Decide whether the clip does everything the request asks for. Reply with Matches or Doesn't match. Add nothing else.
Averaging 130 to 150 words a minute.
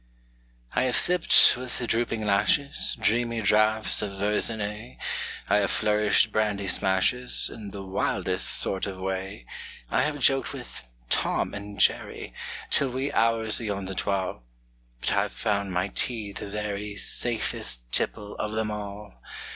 Matches